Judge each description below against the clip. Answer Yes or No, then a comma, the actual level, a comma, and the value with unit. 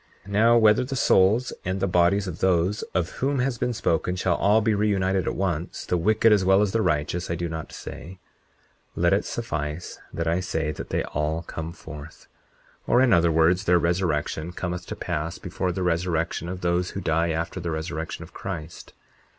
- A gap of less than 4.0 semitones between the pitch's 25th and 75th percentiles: Yes, average, 2.9 semitones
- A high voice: No, very low, 90 Hz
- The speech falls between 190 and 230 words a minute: Yes, average, 200 wpm